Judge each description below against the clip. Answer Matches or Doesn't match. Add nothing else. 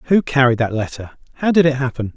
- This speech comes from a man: Matches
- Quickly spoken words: Matches